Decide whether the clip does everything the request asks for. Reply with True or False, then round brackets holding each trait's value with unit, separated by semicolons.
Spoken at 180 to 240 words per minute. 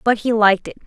False (275 wpm)